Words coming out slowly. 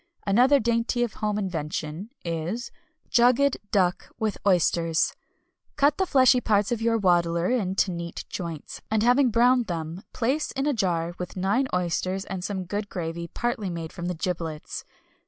No: average, 155 wpm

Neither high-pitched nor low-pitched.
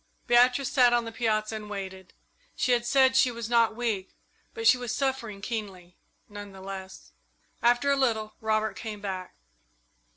No: high, 225 Hz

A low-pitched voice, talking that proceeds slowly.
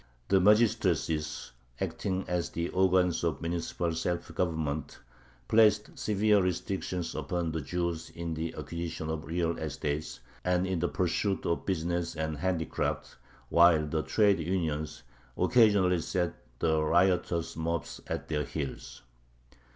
Yes: very low, 85 Hz; slow, 130 wpm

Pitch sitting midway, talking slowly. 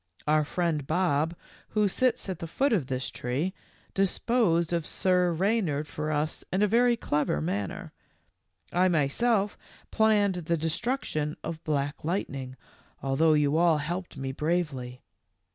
No: medium, 165 Hz; average, 145 wpm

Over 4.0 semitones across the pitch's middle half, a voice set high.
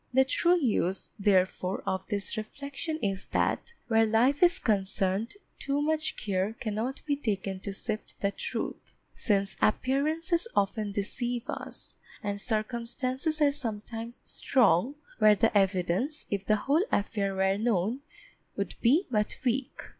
Yes: average, 5.3 semitones; high, 225 Hz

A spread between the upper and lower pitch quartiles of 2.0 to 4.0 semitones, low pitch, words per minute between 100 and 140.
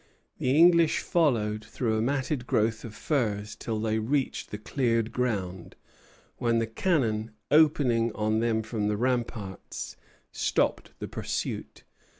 Yes: average, 3.3 semitones; low, 115 Hz; slow, 135 wpm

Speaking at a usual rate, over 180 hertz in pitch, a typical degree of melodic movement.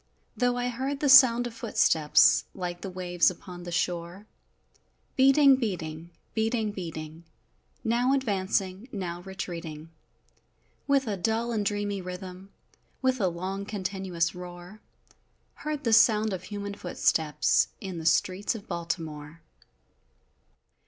No: slow, 125 wpm; high, 190 Hz; average, 4.4 semitones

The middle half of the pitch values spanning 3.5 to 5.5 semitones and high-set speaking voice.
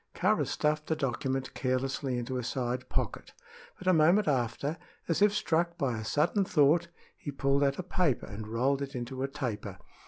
No: average, 4.0 semitones; medium, 140 Hz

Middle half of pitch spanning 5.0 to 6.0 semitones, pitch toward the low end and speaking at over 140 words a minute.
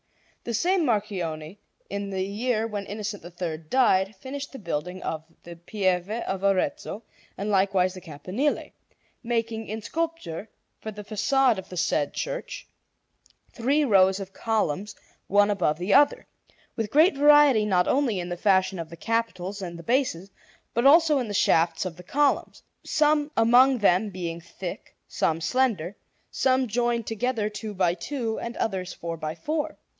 No: wide, 5.4 semitones; high, 205 Hz; average, 160 wpm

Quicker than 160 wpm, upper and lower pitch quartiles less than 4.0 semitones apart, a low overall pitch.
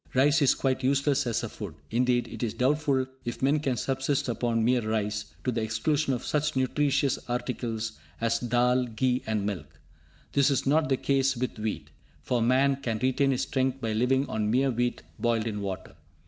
Yes: average, 190 wpm; average, 3.1 semitones; low, 125 Hz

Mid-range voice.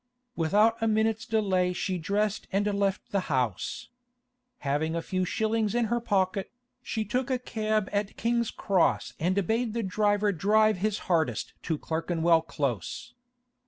No: high, 200 Hz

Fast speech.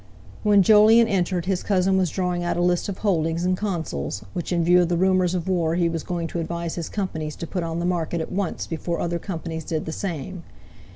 Yes: fast, 230 wpm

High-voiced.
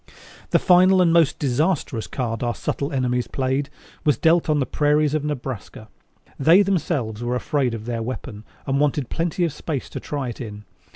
No: medium, 140 Hz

